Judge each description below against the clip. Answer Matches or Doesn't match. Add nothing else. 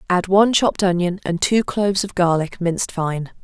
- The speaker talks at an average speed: Matches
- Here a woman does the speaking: Matches